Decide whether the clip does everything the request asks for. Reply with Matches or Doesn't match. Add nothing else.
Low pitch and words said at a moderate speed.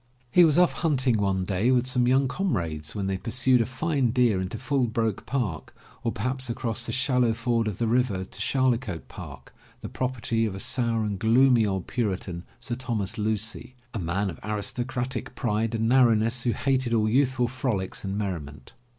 Matches